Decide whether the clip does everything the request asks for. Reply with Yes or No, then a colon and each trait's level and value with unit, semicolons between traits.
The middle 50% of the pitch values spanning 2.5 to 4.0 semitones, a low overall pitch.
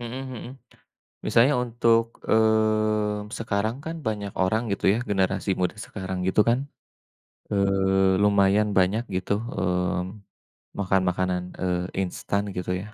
Yes: average, 2.8 semitones; low, 100 Hz